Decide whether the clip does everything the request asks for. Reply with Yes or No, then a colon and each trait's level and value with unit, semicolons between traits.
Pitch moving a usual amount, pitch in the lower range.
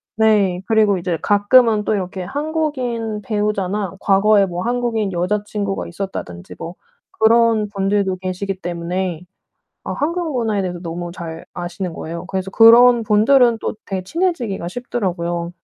No: average, 4.0 semitones; high, 200 Hz